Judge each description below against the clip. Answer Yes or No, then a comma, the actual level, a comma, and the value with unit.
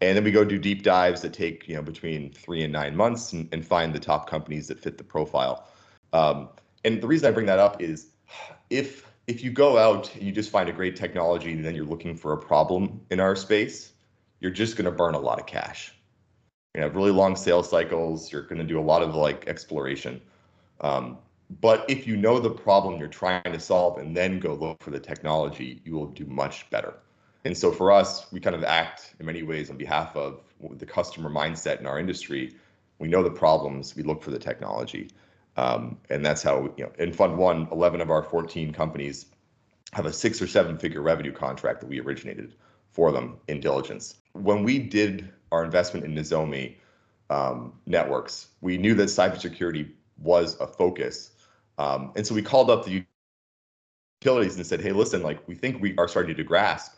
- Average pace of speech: No, fast, 210 wpm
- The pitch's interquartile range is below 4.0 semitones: No, average, 4.5 semitones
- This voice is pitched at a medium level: No, very low, 85 Hz